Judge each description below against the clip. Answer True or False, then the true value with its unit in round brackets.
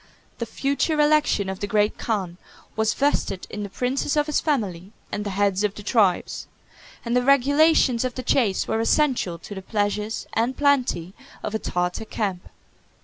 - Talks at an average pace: True (175 wpm)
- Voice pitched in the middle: False (220 Hz)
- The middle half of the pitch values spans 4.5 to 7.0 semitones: True (5.2 semitones)